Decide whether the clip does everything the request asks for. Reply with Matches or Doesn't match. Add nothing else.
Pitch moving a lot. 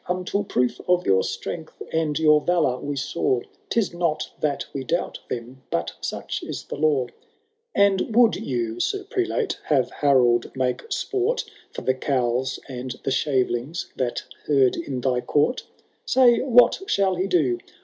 Matches